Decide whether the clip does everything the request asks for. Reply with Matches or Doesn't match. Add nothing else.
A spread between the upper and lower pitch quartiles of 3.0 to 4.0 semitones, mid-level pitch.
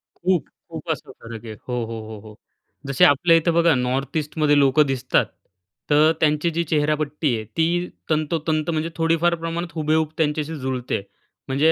Matches